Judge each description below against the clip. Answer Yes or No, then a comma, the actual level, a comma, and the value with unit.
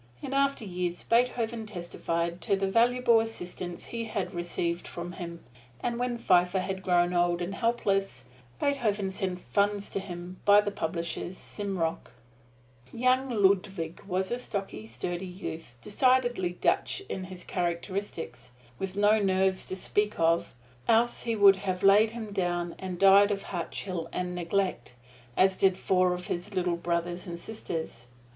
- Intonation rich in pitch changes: No, average, 3.0 semitones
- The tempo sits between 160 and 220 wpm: No, average, 150 wpm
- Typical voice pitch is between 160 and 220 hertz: Yes, high, 190 Hz